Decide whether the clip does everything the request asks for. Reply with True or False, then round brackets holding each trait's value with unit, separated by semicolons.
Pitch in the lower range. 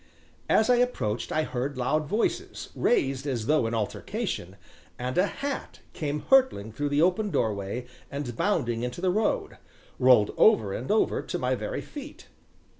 False (145 Hz)